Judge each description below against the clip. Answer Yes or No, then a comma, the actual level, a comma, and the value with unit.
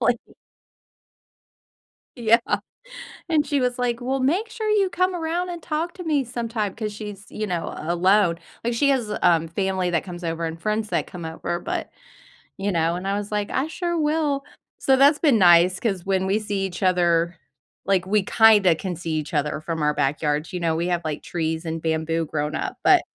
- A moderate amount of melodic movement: No, wide, 7.1 semitones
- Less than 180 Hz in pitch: No, high, 195 Hz